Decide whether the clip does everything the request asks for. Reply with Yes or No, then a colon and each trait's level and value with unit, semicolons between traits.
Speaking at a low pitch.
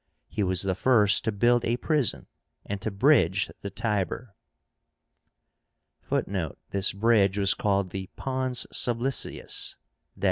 Yes: low, 105 Hz